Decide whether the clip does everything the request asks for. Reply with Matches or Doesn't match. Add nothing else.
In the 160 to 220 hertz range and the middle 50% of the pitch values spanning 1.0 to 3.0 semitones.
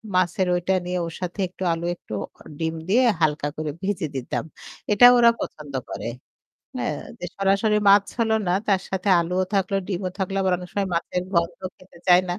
Matches